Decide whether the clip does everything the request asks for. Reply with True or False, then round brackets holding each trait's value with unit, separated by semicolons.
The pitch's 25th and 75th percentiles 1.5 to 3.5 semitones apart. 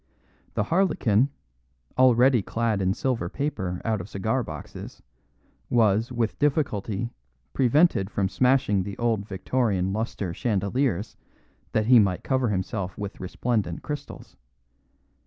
False (4.4 semitones)